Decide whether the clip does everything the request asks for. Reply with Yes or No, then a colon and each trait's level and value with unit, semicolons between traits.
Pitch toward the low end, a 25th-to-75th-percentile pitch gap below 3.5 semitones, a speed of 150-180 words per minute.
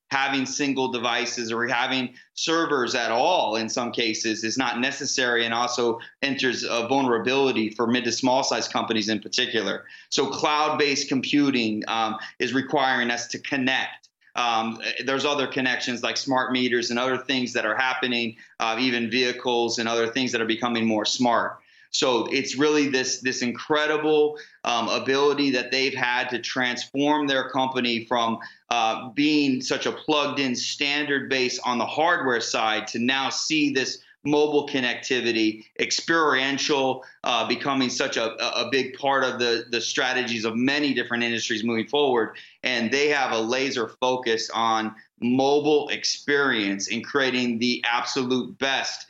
Yes: low, 125 Hz; narrow, 2.6 semitones; average, 155 wpm